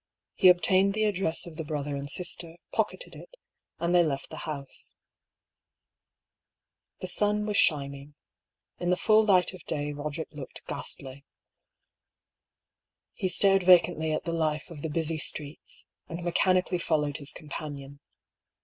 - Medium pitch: Yes, medium, 165 Hz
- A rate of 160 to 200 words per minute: No, average, 140 wpm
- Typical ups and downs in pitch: Yes, average, 3.7 semitones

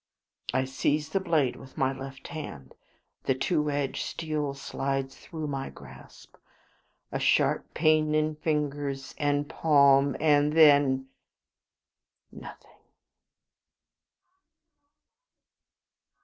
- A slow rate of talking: Yes, slow, 95 wpm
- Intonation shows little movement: Yes, narrow, 2.2 semitones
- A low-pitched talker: No, medium, 145 Hz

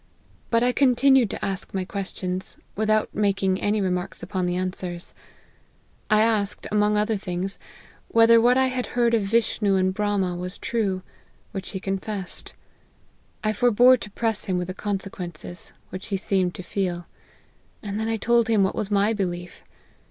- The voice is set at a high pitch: Yes, high, 200 Hz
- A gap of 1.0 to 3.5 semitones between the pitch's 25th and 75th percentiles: Yes, average, 3.1 semitones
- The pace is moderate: Yes, average, 165 wpm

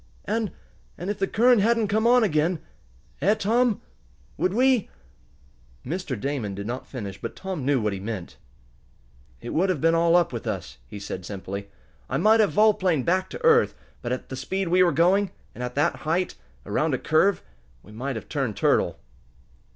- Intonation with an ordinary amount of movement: No, wide, 8.9 semitones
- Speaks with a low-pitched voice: No, medium, 165 Hz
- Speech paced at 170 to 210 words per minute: Yes, average, 190 wpm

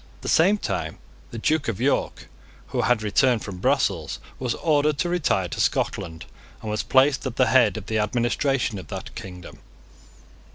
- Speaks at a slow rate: No, average, 175 wpm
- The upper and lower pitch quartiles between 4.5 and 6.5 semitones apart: Yes, average, 5.1 semitones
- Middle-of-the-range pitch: No, low, 120 Hz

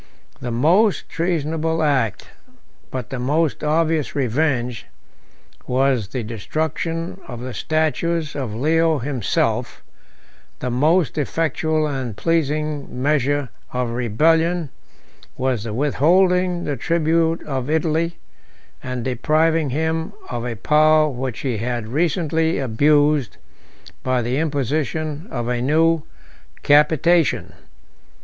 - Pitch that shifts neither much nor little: Yes, average, 4.3 semitones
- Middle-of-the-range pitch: Yes, medium, 150 Hz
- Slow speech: Yes, slow, 110 wpm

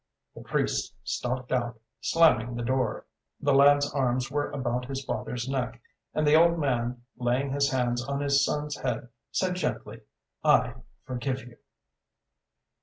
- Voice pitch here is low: Yes, low, 130 Hz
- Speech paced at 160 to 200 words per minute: No, average, 145 wpm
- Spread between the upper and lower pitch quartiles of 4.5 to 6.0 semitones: No, average, 2.7 semitones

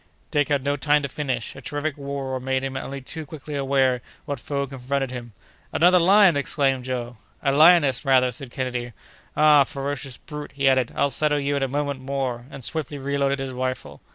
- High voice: No, medium, 140 Hz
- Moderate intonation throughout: No, narrow, 2.0 semitones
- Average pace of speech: Yes, average, 195 wpm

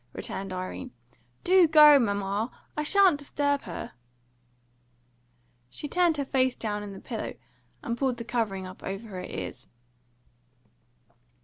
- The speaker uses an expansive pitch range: Yes, wide, 6.9 semitones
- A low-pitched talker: No, high, 235 Hz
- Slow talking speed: Yes, slow, 130 wpm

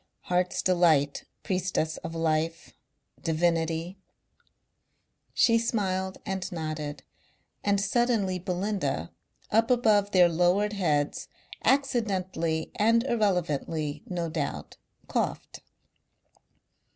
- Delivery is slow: Yes, slow, 85 wpm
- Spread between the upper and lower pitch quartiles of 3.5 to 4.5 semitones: Yes, average, 4.1 semitones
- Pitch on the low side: No, medium, 180 Hz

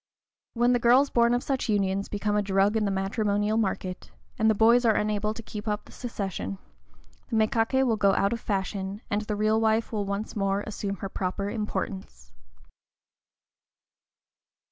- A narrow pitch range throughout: Yes, narrow, 2.2 semitones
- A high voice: Yes, high, 210 Hz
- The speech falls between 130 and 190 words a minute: Yes, average, 170 wpm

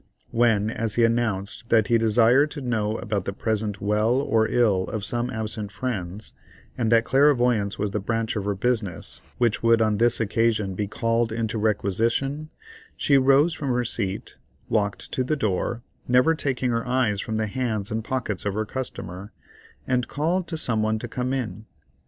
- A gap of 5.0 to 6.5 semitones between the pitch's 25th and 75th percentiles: No, average, 2.9 semitones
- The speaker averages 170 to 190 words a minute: Yes, average, 180 wpm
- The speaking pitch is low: Yes, low, 115 Hz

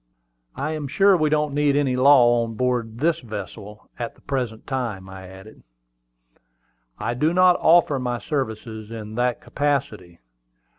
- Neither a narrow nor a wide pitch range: Yes, average, 4.9 semitones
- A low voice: Yes, low, 125 Hz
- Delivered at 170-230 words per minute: No, average, 155 wpm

